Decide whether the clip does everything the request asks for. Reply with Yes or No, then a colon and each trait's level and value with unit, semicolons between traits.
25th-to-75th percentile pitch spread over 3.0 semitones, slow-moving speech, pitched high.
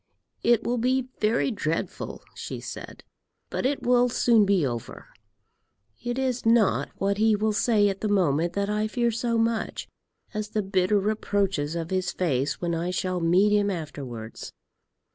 No: average, 4.3 semitones; average, 160 wpm; high, 205 Hz